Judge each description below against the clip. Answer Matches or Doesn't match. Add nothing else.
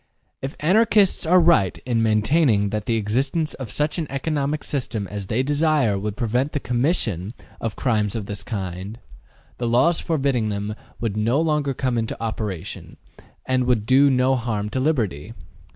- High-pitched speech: Doesn't match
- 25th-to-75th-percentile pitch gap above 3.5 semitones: Matches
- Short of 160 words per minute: Doesn't match